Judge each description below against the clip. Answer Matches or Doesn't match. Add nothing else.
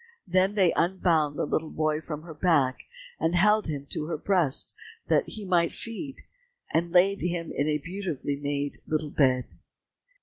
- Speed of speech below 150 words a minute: Doesn't match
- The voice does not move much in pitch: Doesn't match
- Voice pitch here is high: Doesn't match